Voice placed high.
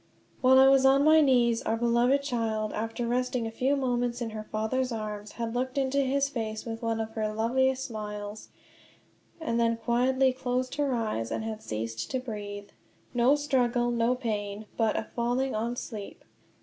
Yes: high, 235 Hz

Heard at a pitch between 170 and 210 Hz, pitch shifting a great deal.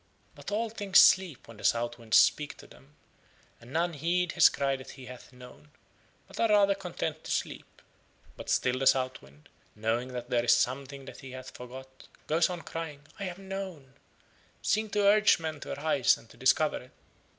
No: medium, 140 Hz; wide, 5.9 semitones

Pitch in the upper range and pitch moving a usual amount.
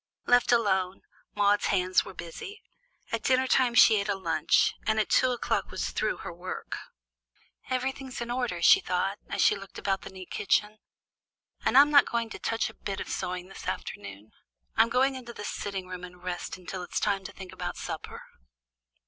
Yes: high, 200 Hz; average, 4.6 semitones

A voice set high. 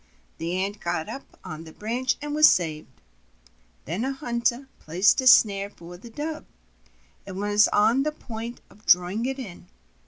Yes: high, 210 Hz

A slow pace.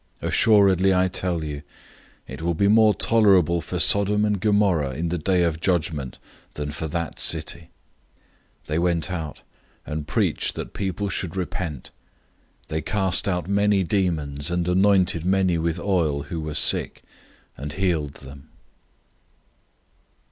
No: average, 145 wpm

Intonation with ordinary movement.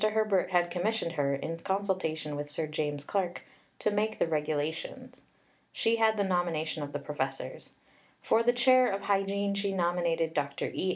Yes: average, 4.9 semitones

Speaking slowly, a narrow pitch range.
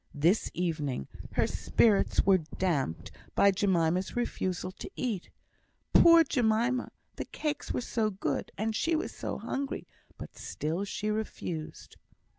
No: slow, 130 wpm; wide, 5.5 semitones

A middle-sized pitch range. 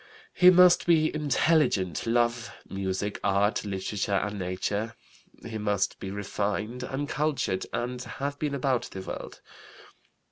No: wide, 6.1 semitones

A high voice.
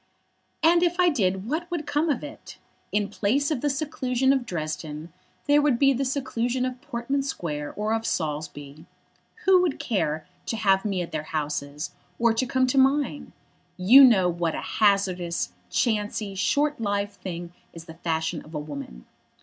Yes: high, 215 Hz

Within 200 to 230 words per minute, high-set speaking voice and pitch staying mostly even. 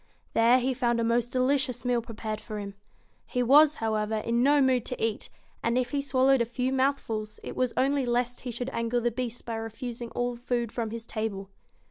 Yes: fast, 205 wpm; high, 240 Hz; narrow, 2.1 semitones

